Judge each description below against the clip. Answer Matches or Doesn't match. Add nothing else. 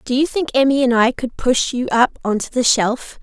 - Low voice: Doesn't match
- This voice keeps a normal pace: Doesn't match